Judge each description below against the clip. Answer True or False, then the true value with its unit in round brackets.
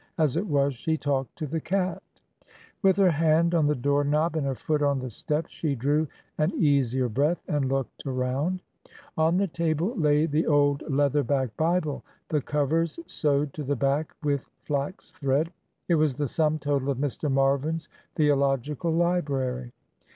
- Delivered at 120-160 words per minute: False (170 wpm)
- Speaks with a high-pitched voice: False (145 Hz)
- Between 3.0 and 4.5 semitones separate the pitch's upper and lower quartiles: False (2.6 semitones)